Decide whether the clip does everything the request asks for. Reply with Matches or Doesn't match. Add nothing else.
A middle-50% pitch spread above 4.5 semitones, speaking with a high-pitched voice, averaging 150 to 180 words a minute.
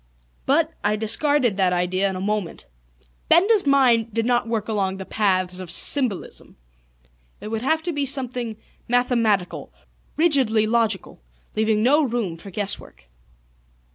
Doesn't match